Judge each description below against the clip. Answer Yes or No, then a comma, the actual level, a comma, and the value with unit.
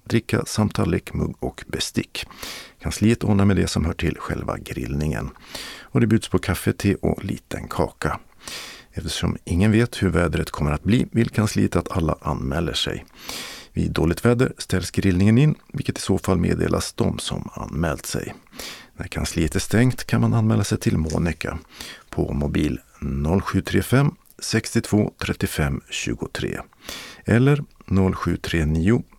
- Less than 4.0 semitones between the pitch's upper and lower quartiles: No, wide, 5.4 semitones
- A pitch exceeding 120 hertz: No, low, 100 Hz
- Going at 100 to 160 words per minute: Yes, average, 145 wpm